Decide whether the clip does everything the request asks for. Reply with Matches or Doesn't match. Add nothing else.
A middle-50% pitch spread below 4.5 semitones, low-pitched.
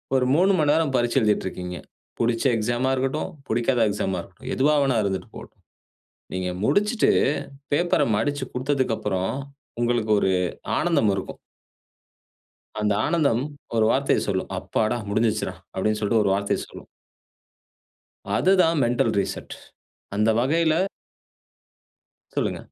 Doesn't match